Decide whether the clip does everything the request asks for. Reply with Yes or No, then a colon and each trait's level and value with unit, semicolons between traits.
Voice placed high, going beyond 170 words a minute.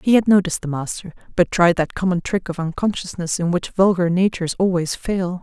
No: medium, 180 Hz; average, 200 wpm